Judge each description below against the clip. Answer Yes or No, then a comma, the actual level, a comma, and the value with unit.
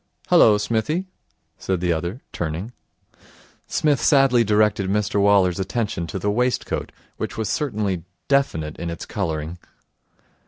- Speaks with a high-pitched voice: No, low, 105 Hz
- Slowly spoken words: Yes, slow, 125 wpm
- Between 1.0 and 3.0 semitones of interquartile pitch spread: No, average, 5.3 semitones